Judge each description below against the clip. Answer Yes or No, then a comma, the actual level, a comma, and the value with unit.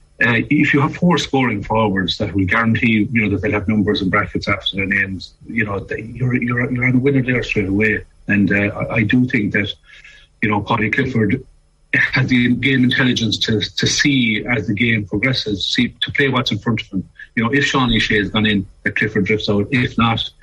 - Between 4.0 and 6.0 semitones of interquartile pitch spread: No, average, 3.6 semitones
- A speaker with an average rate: No, fast, 225 wpm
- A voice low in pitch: Yes, low, 110 Hz